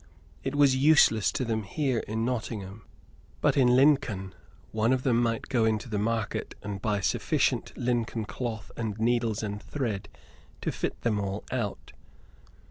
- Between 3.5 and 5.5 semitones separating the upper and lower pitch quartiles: No, average, 3.0 semitones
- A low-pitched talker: Yes, low, 115 Hz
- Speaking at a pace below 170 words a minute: Yes, average, 160 wpm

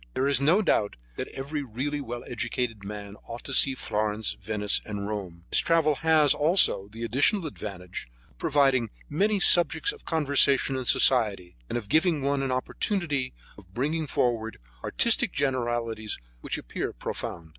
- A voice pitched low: Yes, low, 130 Hz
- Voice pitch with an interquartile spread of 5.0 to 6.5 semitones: Yes, wide, 5.5 semitones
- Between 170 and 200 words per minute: No, average, 155 wpm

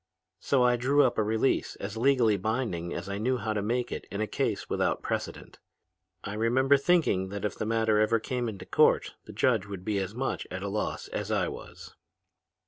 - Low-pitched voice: Yes, low, 110 Hz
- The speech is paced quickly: Yes, fast, 210 wpm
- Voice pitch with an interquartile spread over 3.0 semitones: Yes, average, 3.7 semitones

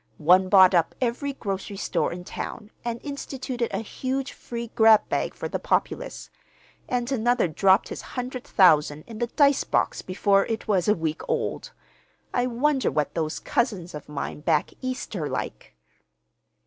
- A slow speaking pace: No, average, 160 wpm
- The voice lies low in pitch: No, high, 220 Hz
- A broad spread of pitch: Yes, wide, 5.7 semitones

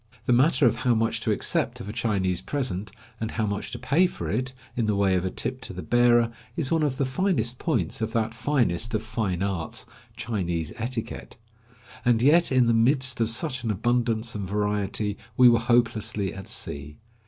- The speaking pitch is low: Yes, low, 115 Hz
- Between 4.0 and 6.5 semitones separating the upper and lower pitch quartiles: No, average, 3.4 semitones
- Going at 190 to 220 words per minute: Yes, average, 200 wpm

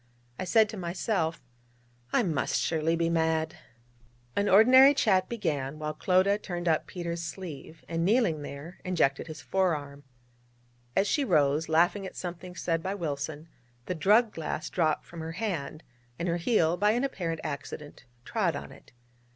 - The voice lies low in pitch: No, medium, 170 Hz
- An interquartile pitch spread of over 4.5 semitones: No, average, 3.5 semitones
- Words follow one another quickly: No, average, 160 wpm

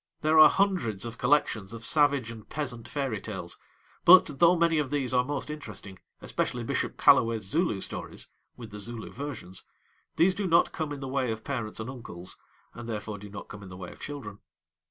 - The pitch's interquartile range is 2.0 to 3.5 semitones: No, wide, 5.4 semitones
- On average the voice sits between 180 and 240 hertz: No, low, 125 Hz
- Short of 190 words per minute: No, average, 195 wpm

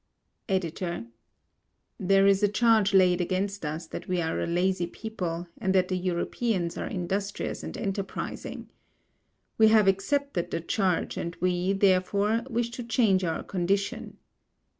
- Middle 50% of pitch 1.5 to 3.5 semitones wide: Yes, average, 2.7 semitones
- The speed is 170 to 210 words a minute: No, average, 140 wpm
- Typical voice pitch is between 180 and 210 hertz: Yes, high, 190 Hz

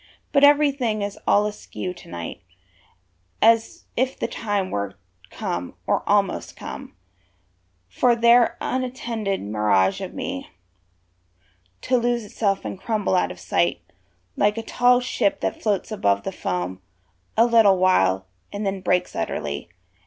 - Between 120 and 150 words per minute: Yes, average, 140 wpm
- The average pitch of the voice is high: Yes, high, 205 Hz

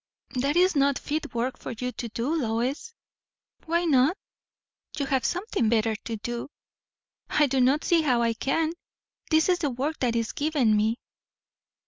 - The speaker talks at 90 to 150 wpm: No, average, 165 wpm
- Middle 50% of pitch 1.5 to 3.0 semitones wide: No, average, 5.0 semitones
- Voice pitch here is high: Yes, very high, 270 Hz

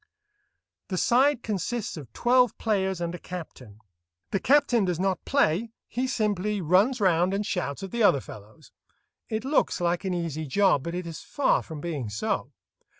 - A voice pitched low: No, high, 190 Hz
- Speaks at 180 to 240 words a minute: No, average, 170 wpm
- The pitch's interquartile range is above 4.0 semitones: Yes, average, 5.2 semitones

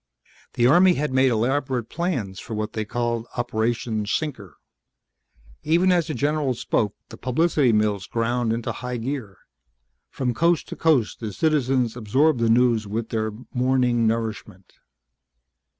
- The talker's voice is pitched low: Yes, low, 120 Hz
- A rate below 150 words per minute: Yes, average, 140 wpm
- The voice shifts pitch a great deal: No, average, 4.0 semitones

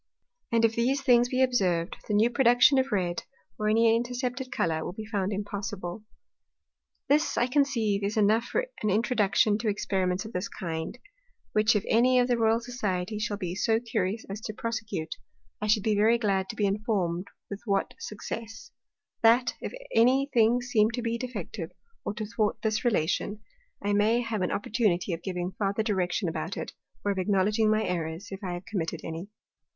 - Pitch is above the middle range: Yes, high, 215 Hz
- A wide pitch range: No, average, 3.3 semitones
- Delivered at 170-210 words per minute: Yes, average, 185 wpm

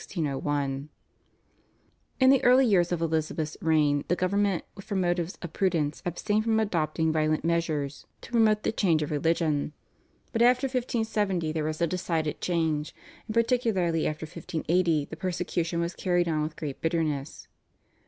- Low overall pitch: No, medium, 170 Hz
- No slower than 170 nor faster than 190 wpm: No, average, 145 wpm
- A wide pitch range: No, average, 4.0 semitones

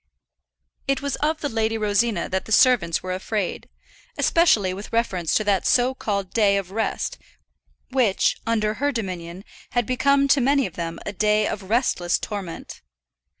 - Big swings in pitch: No, average, 4.7 semitones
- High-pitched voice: Yes, high, 215 Hz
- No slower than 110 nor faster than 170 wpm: Yes, average, 160 wpm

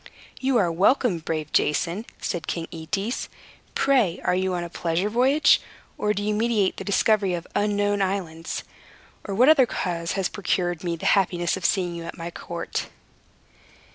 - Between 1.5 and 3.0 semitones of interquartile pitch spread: No, average, 3.6 semitones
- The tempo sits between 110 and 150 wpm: No, average, 170 wpm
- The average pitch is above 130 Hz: Yes, high, 190 Hz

